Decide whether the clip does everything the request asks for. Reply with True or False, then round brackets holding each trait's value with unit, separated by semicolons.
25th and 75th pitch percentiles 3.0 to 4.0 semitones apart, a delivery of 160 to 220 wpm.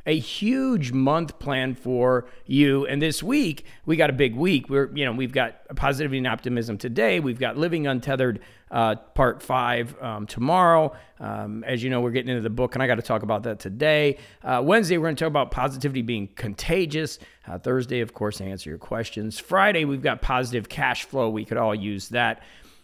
False (4.6 semitones; 200 wpm)